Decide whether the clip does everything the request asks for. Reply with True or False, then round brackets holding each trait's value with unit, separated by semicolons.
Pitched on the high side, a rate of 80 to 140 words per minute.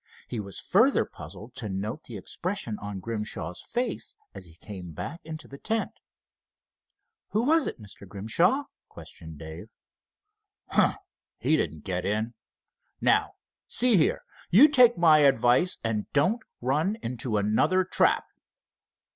False (120 Hz; 135 wpm)